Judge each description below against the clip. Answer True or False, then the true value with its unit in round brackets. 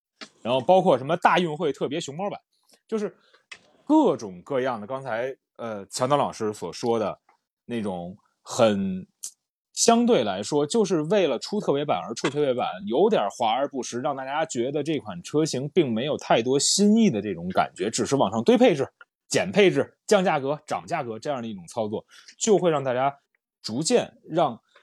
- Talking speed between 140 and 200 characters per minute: False (265 characters per minute)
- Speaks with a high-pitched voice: False (150 Hz)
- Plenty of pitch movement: True (7.9 semitones)